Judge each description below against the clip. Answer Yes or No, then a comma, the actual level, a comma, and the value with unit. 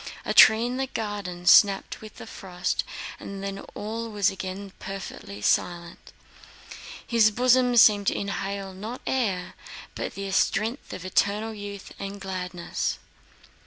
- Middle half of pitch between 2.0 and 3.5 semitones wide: Yes, narrow, 2.4 semitones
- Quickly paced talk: No, slow, 135 wpm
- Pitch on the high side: Yes, high, 200 Hz